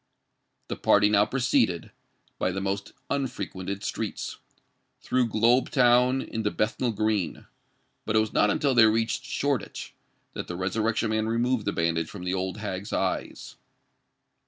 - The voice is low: Yes, low, 110 Hz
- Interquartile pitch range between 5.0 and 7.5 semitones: No, average, 3.6 semitones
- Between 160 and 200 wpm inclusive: No, average, 145 wpm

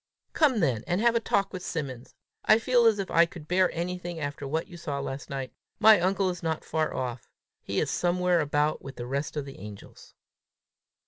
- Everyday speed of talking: No, fast, 210 wpm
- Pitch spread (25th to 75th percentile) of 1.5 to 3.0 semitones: No, average, 4.9 semitones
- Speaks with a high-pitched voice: No, medium, 170 Hz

